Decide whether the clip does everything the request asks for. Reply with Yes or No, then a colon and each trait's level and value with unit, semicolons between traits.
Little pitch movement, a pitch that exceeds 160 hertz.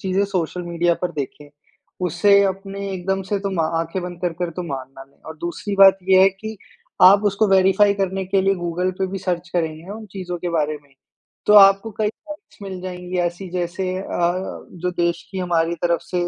Yes: narrow, 2.1 semitones; medium, 185 Hz